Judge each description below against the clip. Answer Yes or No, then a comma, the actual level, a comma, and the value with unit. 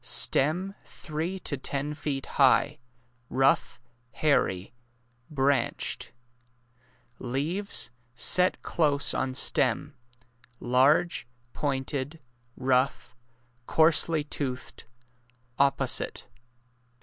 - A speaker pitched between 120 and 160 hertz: Yes, medium, 140 Hz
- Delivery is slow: Yes, slow, 75 wpm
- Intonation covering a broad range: No, average, 3.2 semitones